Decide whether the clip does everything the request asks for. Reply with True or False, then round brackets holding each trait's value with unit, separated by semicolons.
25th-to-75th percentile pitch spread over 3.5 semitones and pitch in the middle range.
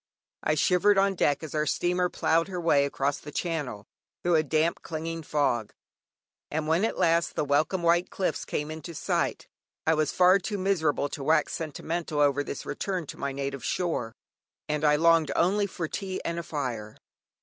False (3.2 semitones; 160 Hz)